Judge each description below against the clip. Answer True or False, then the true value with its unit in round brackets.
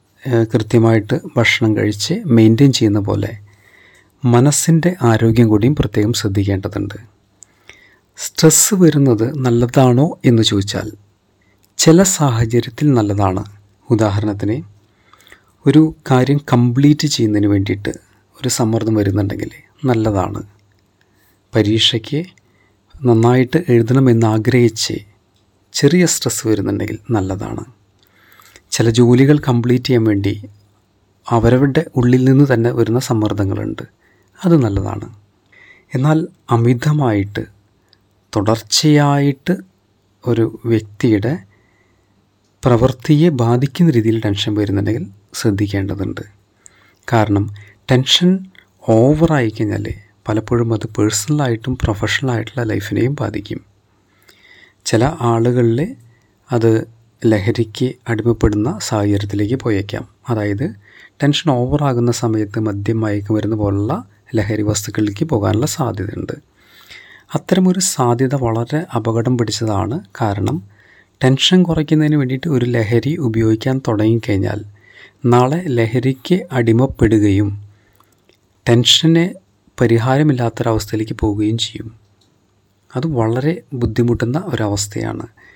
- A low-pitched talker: True (115 Hz)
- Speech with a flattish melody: False (3.6 semitones)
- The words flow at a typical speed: True (80 wpm)